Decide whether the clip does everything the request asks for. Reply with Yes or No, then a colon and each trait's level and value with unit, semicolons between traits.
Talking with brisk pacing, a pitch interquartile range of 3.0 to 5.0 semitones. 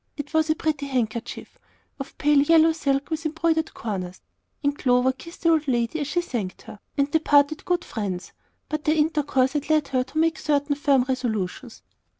No: average, 185 wpm; average, 3.7 semitones